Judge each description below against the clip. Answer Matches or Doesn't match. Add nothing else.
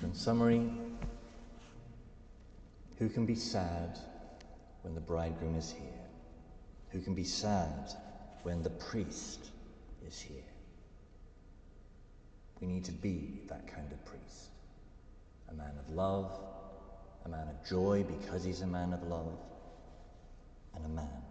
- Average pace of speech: Doesn't match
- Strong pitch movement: Doesn't match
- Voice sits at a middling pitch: Doesn't match